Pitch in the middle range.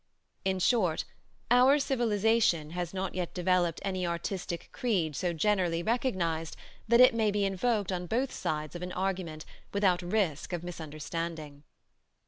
Yes: medium, 180 Hz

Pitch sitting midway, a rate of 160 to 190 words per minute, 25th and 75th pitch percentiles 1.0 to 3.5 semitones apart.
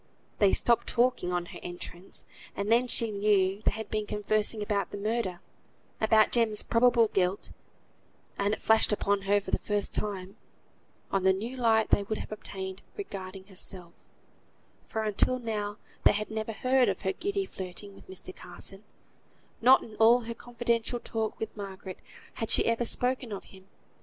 No: high, 210 Hz; average, 170 wpm; average, 2.9 semitones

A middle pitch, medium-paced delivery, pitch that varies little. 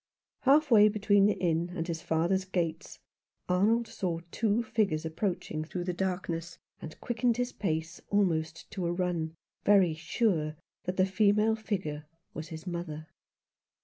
No: medium, 180 Hz; average, 145 wpm; average, 4.1 semitones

